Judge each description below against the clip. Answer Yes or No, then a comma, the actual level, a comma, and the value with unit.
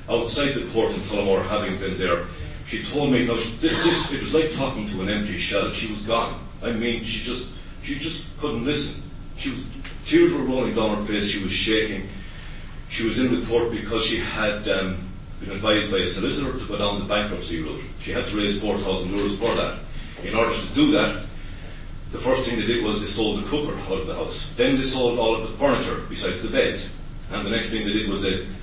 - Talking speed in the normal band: No, fast, 230 wpm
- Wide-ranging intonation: No, average, 3.6 semitones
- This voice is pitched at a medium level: No, low, 105 Hz